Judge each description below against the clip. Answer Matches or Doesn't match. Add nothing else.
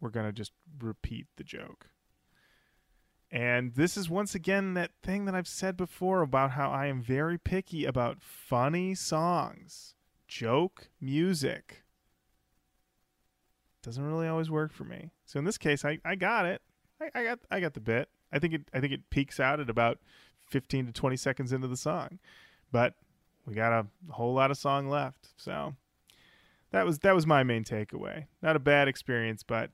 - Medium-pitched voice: Matches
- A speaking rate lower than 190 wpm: Matches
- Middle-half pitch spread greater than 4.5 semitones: Matches